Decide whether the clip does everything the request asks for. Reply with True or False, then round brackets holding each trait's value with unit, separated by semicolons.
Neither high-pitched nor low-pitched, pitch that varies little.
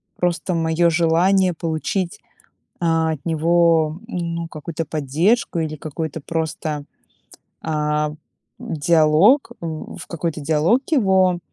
True (165 Hz; 2.0 semitones)